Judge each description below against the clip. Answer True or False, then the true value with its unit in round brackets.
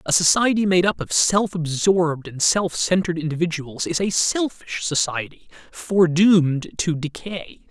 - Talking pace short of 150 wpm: True (140 wpm)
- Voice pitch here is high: False (170 Hz)